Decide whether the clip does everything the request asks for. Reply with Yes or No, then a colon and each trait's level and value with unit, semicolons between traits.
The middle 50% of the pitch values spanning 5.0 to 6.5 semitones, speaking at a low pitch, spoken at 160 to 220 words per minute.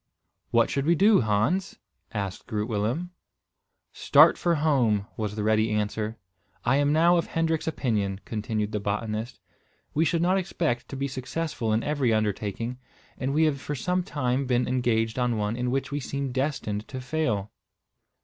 Yes: wide, 5.6 semitones; low, 125 Hz; average, 170 wpm